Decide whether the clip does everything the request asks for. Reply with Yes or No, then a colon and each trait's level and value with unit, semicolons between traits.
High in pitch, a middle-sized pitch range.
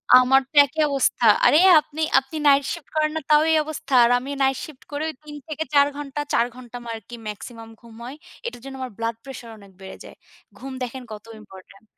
Yes: very high, 270 Hz; average, 4.1 semitones